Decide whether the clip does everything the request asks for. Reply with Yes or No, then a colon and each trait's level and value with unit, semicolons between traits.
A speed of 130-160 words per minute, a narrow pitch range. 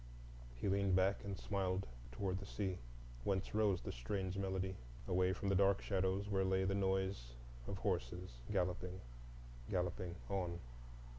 Yes: average, 145 wpm; narrow, 1.2 semitones